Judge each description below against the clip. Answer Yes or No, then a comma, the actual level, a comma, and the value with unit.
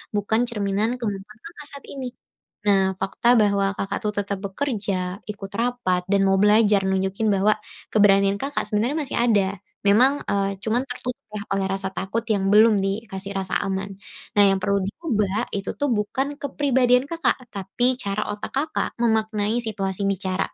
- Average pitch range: Yes, average, 3.3 semitones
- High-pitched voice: Yes, high, 205 Hz